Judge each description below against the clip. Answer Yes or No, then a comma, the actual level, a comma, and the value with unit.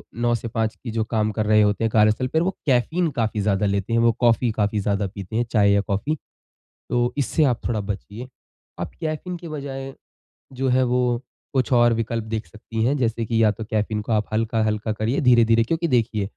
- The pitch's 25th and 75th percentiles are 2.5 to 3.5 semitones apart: Yes, average, 2.8 semitones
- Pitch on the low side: Yes, low, 115 Hz